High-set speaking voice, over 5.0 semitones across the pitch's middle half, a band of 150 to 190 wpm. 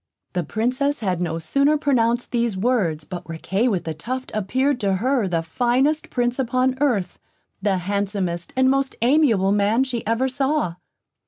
Yes: high, 230 Hz; wide, 5.6 semitones; average, 160 wpm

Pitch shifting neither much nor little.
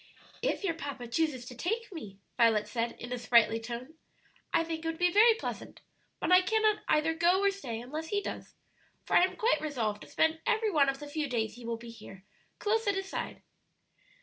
No: wide, 7.9 semitones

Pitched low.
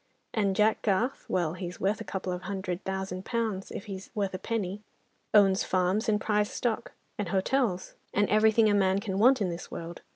No: high, 195 Hz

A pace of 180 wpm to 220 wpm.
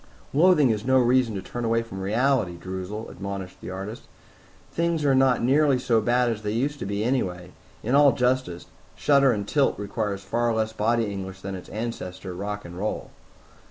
Yes: average, 185 wpm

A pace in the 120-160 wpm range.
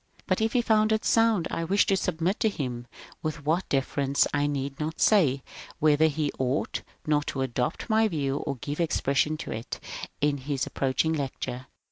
No: average, 185 wpm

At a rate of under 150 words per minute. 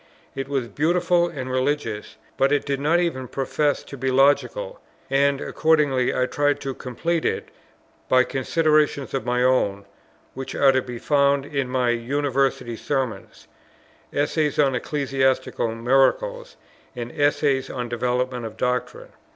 Yes: average, 140 wpm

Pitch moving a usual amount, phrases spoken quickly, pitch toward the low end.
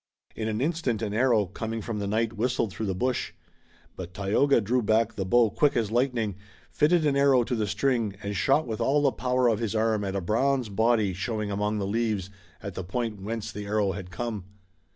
Yes: average, 3.2 semitones; fast, 215 wpm; low, 110 Hz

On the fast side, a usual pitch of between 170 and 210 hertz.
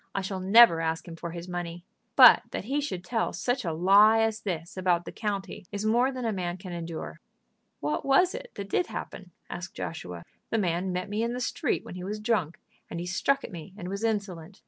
Yes: fast, 225 wpm; high, 190 Hz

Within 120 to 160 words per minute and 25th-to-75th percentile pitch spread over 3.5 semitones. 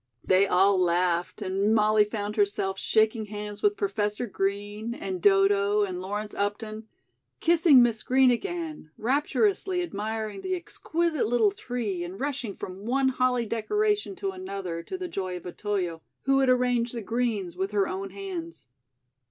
Yes: average, 150 wpm; average, 4.5 semitones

